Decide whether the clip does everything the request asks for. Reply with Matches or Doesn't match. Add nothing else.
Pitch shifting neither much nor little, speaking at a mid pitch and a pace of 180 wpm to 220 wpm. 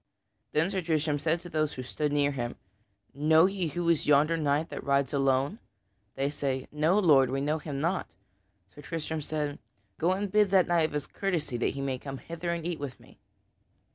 Matches